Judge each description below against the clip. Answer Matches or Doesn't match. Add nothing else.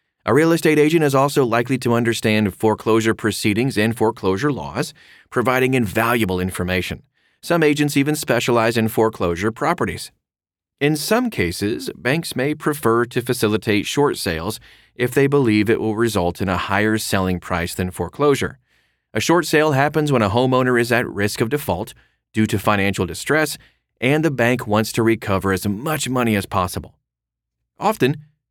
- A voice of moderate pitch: Doesn't match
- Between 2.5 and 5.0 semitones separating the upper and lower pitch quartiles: Doesn't match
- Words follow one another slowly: Doesn't match